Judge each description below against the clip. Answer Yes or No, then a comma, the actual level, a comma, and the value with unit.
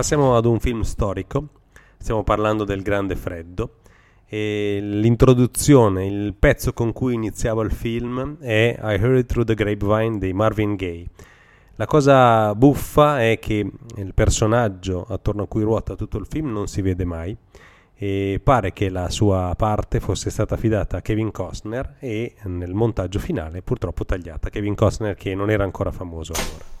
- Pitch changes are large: No, average, 3.2 semitones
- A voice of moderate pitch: No, low, 105 Hz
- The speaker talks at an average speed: Yes, average, 160 wpm